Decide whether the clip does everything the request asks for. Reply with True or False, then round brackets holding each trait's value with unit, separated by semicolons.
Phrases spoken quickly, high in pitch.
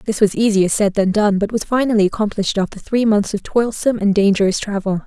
True (215 wpm; 210 Hz)